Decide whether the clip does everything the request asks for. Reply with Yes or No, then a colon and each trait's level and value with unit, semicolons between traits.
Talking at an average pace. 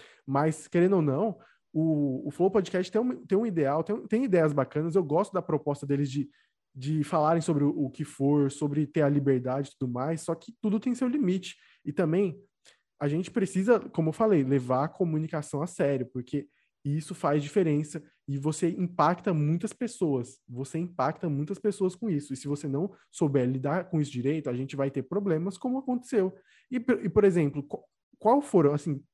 No: fast, 195 wpm